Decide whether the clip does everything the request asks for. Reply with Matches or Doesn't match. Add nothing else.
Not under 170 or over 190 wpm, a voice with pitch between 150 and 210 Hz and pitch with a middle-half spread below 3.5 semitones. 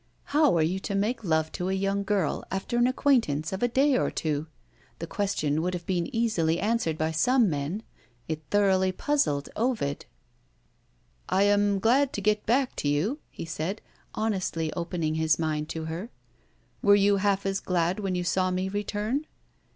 Doesn't match